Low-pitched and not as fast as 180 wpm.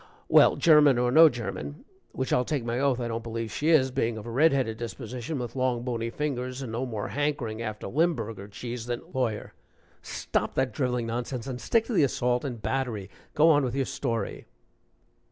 No: low, 125 Hz; average, 200 wpm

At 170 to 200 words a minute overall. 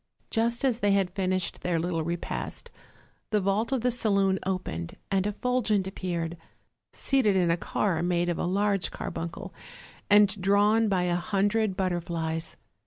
No: average, 155 wpm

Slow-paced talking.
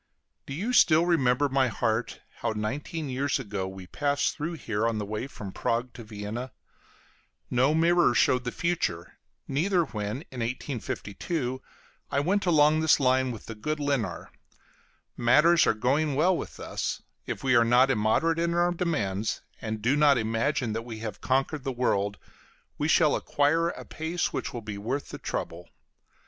No: average, 170 wpm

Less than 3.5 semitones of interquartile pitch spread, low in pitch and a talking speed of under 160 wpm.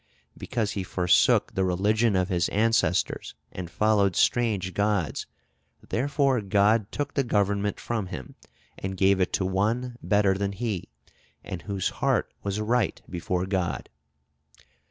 Yes: average, 2.9 semitones; low, 100 Hz; slow, 135 wpm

